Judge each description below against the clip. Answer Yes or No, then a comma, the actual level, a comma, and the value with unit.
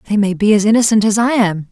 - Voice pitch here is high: Yes, high, 210 Hz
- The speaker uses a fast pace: Yes, fast, 280 wpm